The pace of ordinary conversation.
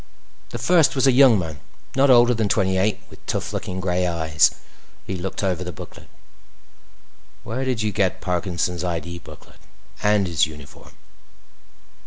Yes: average, 155 wpm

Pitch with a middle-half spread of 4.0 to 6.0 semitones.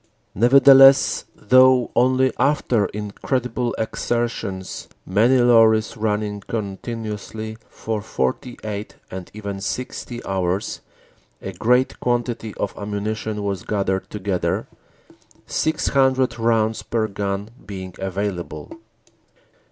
No: average, 3.3 semitones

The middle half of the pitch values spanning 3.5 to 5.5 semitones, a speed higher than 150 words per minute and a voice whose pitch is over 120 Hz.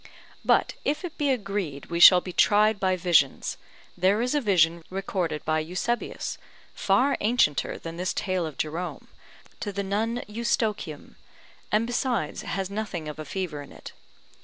Yes: average, 4.7 semitones; average, 160 wpm; high, 190 Hz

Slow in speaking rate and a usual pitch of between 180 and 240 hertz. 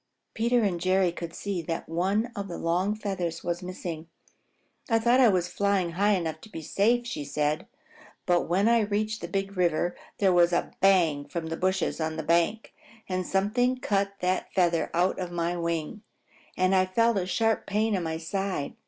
No: average, 190 wpm; medium, 185 Hz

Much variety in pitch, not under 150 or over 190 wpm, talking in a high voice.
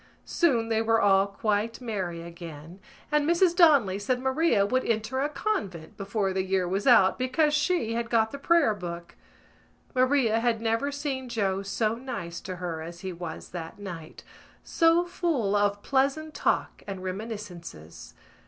Yes: wide, 5.8 semitones; average, 160 wpm; high, 220 Hz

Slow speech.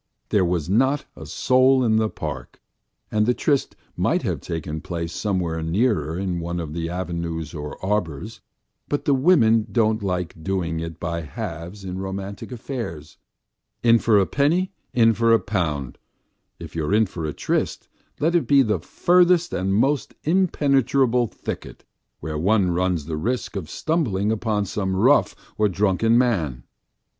No: average, 160 wpm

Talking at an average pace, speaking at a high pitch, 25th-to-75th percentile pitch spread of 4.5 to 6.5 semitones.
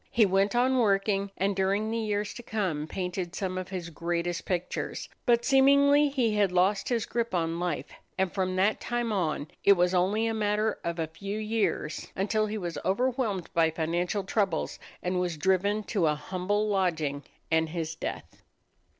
No: average, 175 wpm; high, 195 Hz; average, 3.6 semitones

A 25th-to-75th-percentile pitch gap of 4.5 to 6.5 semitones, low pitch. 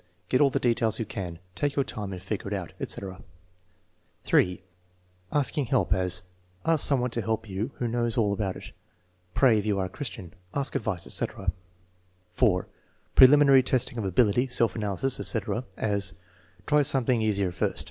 Yes: average, 4.9 semitones; low, 110 Hz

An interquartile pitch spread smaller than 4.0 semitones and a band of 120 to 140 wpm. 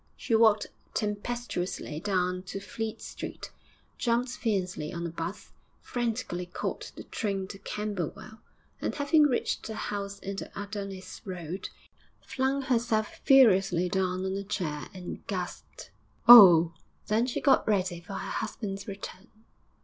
Yes: average, 3.6 semitones; slow, 135 wpm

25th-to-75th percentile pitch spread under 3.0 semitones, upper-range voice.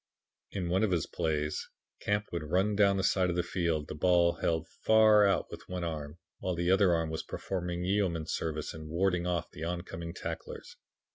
No: narrow, 2.6 semitones; very low, 85 Hz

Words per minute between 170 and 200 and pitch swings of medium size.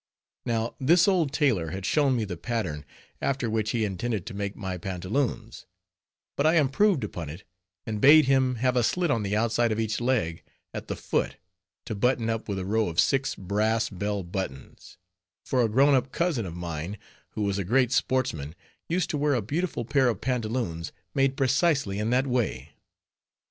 Yes: average, 185 wpm; average, 5.0 semitones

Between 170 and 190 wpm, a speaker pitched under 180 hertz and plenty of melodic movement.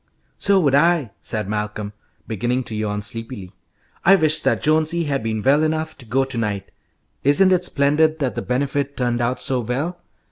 Yes: average, 180 wpm; low, 135 Hz; wide, 5.7 semitones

